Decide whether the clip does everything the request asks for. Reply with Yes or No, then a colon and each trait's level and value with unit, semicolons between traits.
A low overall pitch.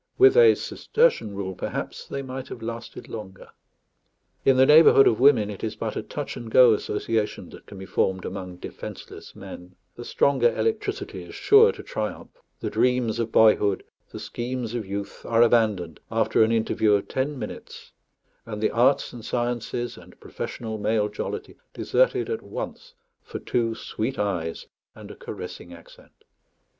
Yes: low, 115 Hz